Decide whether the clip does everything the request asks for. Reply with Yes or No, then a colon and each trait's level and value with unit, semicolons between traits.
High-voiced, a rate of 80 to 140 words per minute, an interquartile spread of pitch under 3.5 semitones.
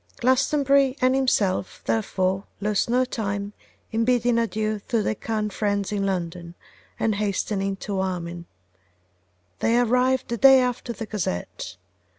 No: high, 215 Hz; slow, 135 wpm; average, 4.0 semitones